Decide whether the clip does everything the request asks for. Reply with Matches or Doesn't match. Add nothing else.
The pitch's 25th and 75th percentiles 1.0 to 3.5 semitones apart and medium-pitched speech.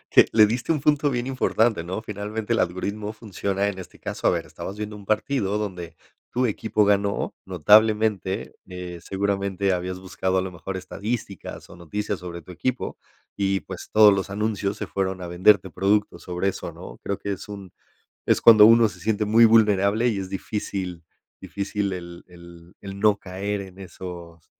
Doesn't match